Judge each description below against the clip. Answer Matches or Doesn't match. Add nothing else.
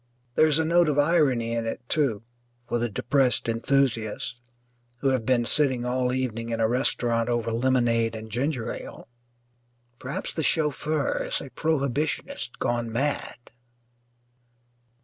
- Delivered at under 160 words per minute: Matches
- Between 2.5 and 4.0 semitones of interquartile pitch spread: Matches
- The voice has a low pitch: Matches